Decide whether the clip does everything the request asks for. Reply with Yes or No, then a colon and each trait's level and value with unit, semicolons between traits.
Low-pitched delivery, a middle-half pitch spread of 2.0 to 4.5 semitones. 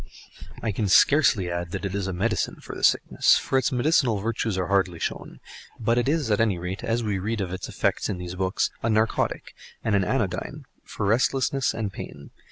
Yes: low, 105 Hz; average, 3.7 semitones